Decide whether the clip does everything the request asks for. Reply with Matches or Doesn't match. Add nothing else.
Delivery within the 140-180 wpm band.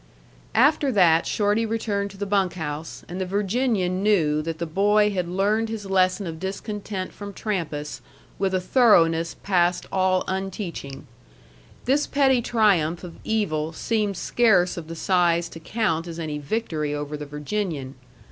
Matches